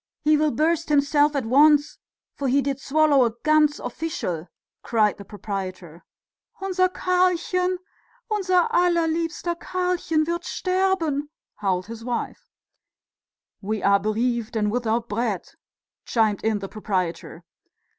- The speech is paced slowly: Yes, slow, 120 wpm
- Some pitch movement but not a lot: No, wide, 7.6 semitones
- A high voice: Yes, very high, 280 Hz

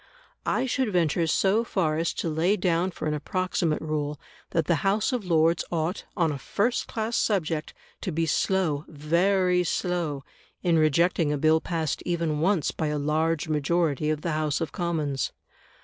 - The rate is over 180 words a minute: No, average, 170 wpm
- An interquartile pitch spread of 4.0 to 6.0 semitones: No, average, 3.0 semitones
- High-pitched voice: No, medium, 165 Hz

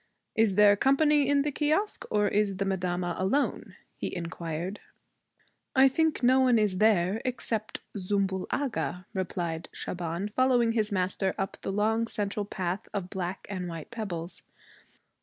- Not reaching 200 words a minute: Yes, average, 140 wpm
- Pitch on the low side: No, high, 205 Hz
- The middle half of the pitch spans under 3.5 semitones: No, average, 4.4 semitones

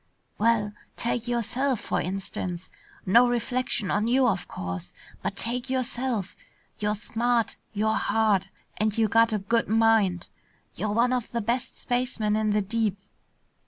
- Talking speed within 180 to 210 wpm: No, average, 145 wpm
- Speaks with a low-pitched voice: No, high, 225 Hz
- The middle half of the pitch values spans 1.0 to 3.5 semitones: Yes, average, 2.7 semitones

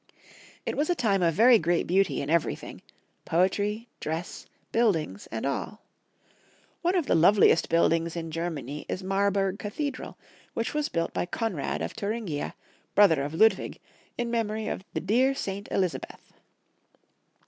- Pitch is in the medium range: No, high, 195 Hz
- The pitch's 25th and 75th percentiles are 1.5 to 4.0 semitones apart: No, average, 5.2 semitones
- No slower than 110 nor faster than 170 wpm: Yes, average, 155 wpm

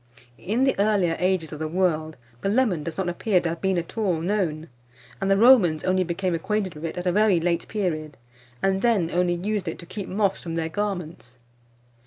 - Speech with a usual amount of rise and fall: Yes, average, 3.3 semitones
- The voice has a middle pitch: Yes, medium, 180 Hz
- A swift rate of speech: Yes, fast, 210 wpm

